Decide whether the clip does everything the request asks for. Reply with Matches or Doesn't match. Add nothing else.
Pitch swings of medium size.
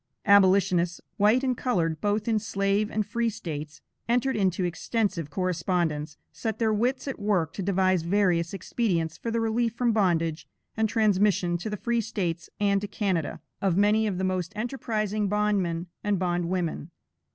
Matches